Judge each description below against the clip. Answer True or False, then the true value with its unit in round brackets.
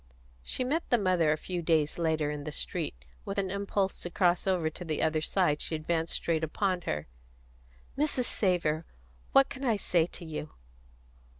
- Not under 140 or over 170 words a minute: False (180 wpm)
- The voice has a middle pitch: True (170 Hz)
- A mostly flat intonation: False (3.9 semitones)